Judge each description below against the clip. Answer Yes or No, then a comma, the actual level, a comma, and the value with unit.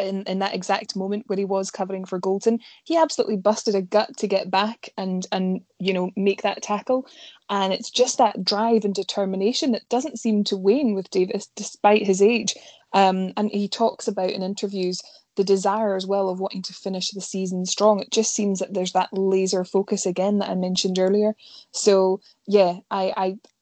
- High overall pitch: Yes, high, 200 Hz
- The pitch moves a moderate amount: No, narrow, 1.9 semitones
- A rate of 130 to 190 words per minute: No, average, 200 wpm